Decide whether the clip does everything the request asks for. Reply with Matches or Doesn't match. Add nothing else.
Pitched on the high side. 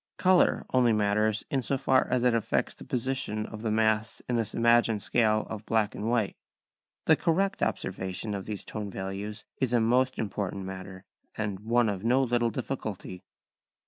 Doesn't match